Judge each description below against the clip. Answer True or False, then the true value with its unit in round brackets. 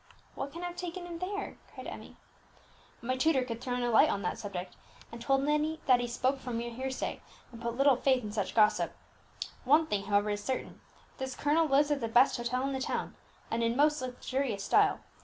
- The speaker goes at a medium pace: False (210 wpm)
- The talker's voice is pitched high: True (255 Hz)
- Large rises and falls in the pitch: False (3.8 semitones)